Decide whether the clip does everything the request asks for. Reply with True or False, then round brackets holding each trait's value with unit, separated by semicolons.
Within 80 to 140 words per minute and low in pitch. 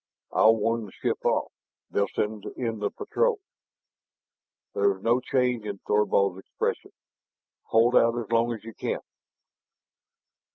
True (135 wpm; 115 Hz)